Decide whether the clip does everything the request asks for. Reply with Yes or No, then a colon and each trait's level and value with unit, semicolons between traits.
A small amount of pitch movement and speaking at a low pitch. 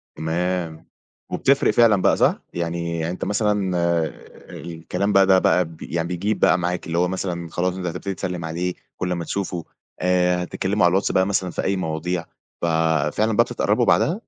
Yes: narrow, 2.0 semitones; very low, 90 Hz